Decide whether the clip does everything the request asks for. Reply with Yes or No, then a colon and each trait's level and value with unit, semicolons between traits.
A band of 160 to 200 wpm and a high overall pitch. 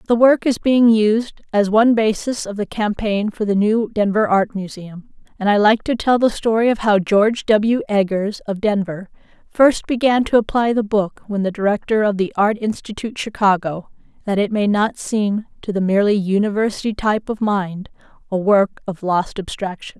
Yes: average, 185 wpm; high, 210 Hz